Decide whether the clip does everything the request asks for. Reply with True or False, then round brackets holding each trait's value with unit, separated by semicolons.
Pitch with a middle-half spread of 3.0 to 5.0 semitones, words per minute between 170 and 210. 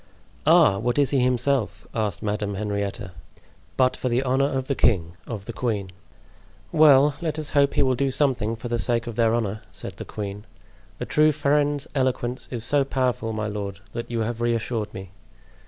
True (4.2 semitones; 185 wpm)